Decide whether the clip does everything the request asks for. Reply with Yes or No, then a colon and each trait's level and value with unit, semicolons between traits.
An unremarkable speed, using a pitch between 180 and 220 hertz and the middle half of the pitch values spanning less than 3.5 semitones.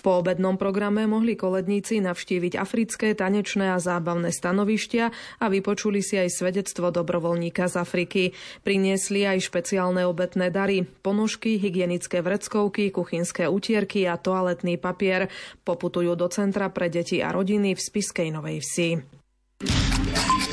Yes: average, 125 wpm; high, 190 Hz; narrow, 2.4 semitones